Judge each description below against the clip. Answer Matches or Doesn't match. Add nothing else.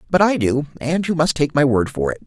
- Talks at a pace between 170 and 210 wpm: Doesn't match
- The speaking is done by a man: Matches